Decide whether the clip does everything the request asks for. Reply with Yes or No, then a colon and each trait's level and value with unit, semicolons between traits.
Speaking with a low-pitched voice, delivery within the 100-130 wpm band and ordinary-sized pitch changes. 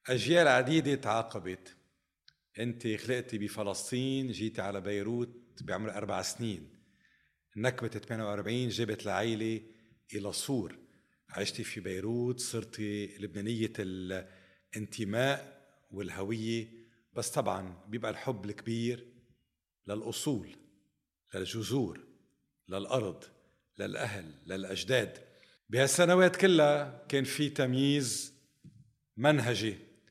No: low, 115 Hz; average, 80 wpm; average, 3.7 semitones